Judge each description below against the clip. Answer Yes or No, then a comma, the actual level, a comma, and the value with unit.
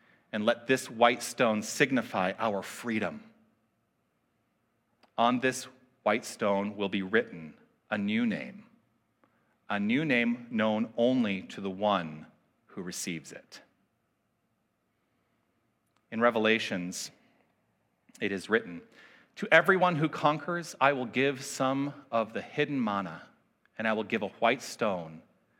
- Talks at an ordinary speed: No, slow, 125 wpm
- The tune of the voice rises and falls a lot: Yes, wide, 5.9 semitones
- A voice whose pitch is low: Yes, low, 115 Hz